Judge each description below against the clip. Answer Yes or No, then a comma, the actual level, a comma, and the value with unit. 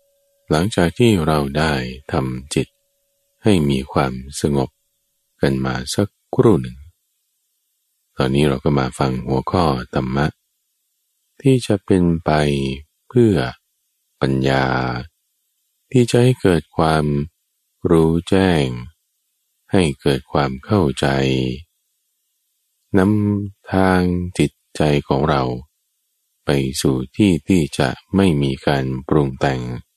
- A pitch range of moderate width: No, wide, 6.5 semitones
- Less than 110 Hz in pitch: Yes, very low, 75 Hz